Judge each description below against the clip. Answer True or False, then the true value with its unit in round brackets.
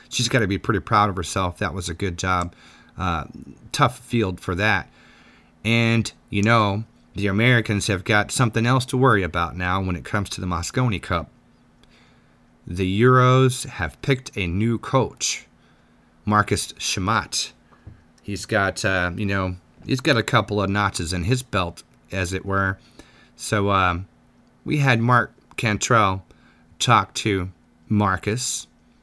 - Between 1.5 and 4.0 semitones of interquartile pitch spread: False (4.4 semitones)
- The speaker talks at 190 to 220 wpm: False (150 wpm)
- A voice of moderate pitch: False (100 Hz)